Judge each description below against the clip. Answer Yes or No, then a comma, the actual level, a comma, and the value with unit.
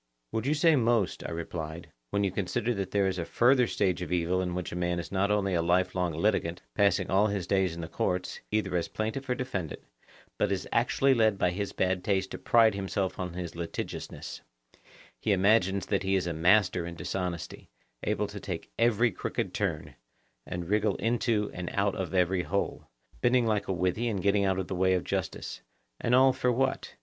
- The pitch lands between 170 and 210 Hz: No, very low, 95 Hz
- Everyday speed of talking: No, fast, 210 wpm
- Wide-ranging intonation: No, average, 3.3 semitones